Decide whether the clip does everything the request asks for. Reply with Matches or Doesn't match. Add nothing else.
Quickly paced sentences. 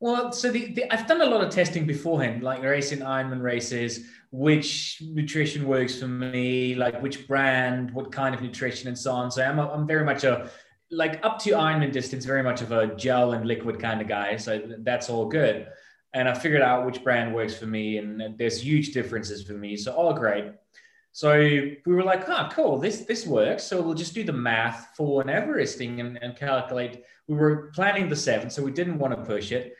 Matches